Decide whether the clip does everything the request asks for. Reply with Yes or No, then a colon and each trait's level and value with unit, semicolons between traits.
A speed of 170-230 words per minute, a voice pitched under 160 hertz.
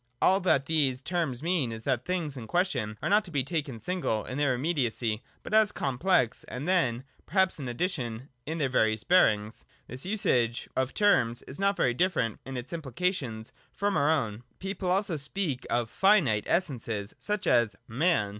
Yes: average, 185 wpm; medium, 140 Hz